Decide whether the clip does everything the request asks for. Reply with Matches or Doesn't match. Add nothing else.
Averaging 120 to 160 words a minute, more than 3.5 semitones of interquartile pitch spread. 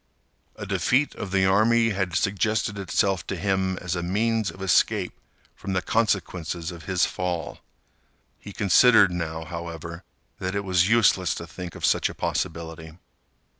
Doesn't match